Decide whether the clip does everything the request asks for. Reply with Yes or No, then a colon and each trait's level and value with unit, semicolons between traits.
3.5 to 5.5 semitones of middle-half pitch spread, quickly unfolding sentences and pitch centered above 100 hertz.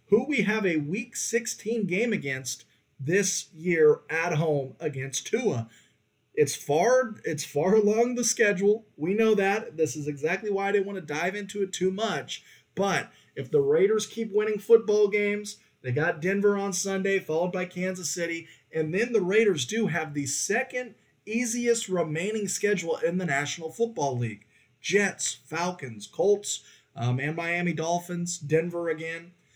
No: average, 5.1 semitones; average, 160 wpm; medium, 185 Hz